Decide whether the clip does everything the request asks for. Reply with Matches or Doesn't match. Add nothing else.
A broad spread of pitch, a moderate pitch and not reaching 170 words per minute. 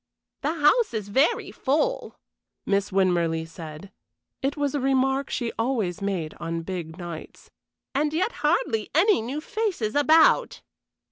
Doesn't match